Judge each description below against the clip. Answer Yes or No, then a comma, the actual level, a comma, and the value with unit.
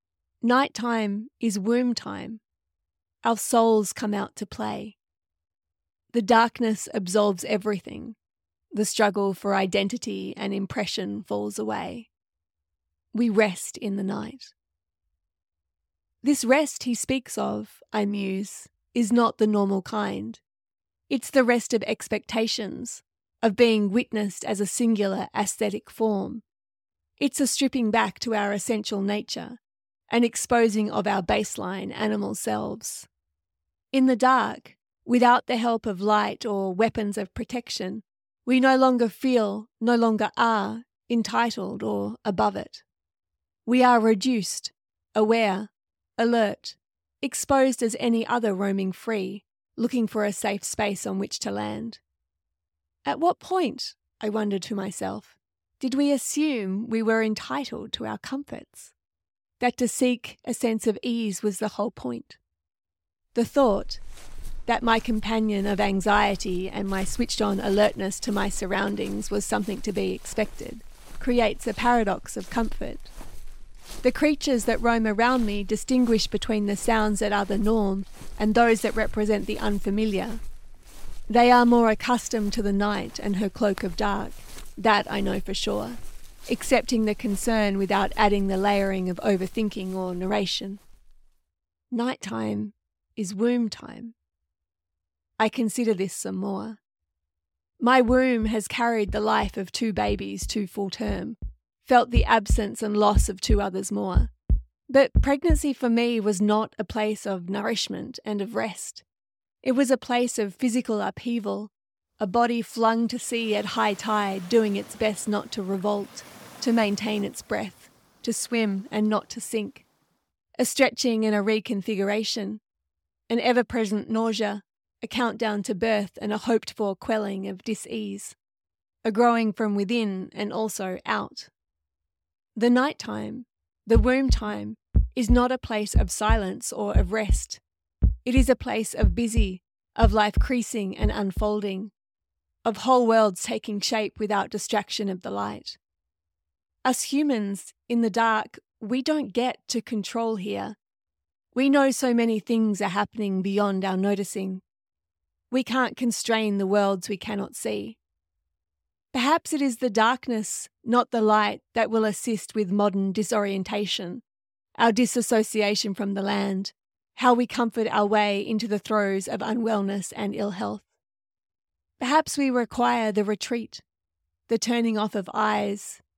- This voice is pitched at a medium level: No, high, 215 Hz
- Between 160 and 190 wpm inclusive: No, average, 140 wpm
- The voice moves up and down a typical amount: Yes, average, 3.2 semitones